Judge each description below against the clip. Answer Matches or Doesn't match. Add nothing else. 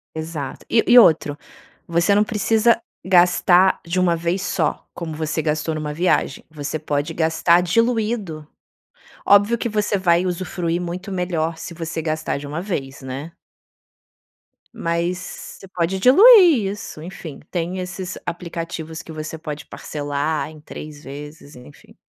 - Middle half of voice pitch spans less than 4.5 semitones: Matches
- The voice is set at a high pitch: Doesn't match